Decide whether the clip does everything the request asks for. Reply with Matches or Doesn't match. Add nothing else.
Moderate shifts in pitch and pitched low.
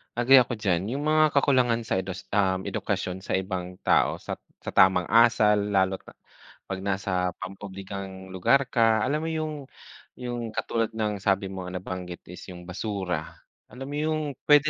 Matches